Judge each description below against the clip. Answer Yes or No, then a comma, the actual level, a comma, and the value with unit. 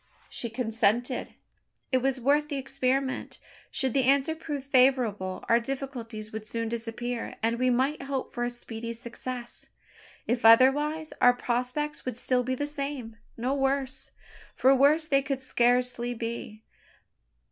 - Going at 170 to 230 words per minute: No, average, 145 wpm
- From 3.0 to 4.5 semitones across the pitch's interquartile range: No, narrow, 2.6 semitones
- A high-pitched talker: Yes, very high, 250 Hz